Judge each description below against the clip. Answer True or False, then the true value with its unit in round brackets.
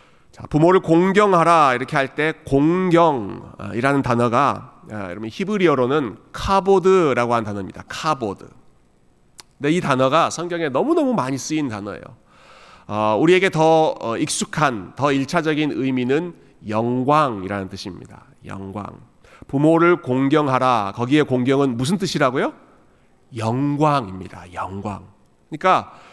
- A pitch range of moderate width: False (6.8 semitones)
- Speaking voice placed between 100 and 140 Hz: True (135 Hz)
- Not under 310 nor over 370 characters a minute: False (280 characters per minute)